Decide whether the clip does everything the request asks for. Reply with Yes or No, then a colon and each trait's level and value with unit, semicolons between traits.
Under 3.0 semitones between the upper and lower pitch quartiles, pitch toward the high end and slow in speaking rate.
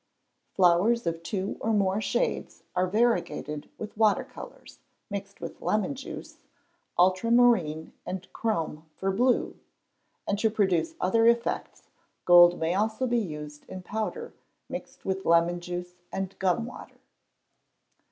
No: average, 4.3 semitones; high, 195 Hz; slow, 130 wpm